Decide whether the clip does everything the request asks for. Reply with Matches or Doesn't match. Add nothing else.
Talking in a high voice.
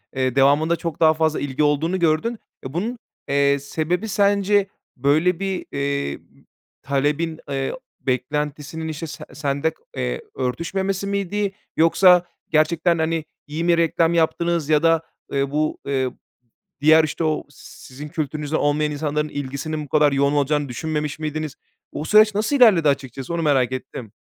Doesn't match